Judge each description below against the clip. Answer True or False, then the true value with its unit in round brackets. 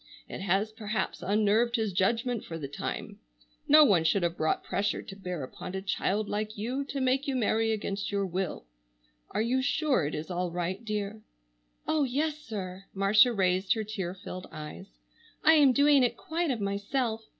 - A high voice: True (210 Hz)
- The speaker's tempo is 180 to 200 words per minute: True (185 wpm)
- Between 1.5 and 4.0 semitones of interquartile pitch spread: False (4.7 semitones)